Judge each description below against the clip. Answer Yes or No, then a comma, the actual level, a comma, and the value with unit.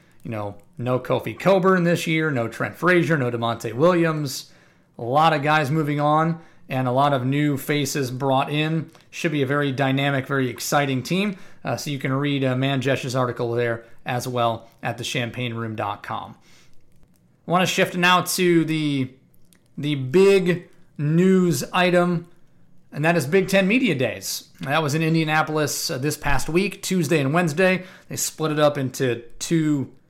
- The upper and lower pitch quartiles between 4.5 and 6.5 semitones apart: Yes, average, 4.8 semitones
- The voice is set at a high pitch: No, medium, 150 Hz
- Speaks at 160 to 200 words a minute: Yes, average, 165 wpm